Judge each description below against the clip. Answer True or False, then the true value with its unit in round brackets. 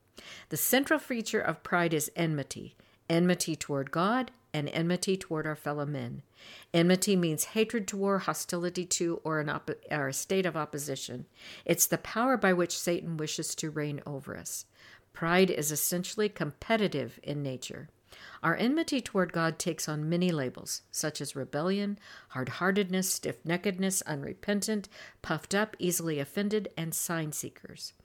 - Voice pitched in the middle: True (170 Hz)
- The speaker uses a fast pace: False (150 wpm)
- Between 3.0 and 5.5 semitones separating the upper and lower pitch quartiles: True (4.2 semitones)